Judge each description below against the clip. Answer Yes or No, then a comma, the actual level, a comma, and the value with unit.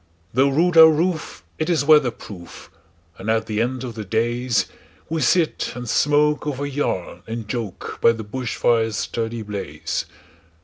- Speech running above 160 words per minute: No, average, 145 wpm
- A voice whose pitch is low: Yes, low, 120 Hz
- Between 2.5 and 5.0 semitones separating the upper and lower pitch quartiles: No, wide, 5.5 semitones